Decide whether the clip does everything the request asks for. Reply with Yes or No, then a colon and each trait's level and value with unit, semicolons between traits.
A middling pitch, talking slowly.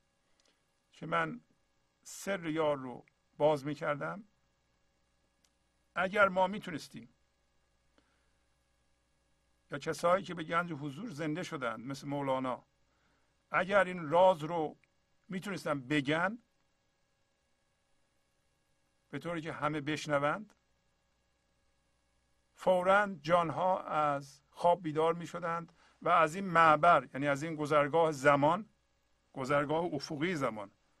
Yes: medium, 150 Hz; slow, 95 wpm